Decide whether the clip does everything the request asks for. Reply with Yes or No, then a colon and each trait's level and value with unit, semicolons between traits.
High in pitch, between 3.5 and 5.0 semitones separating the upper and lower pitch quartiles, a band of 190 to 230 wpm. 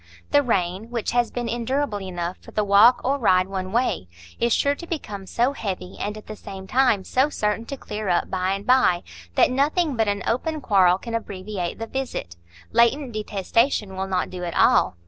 Yes: high, 215 Hz; average, 4.7 semitones; average, 200 wpm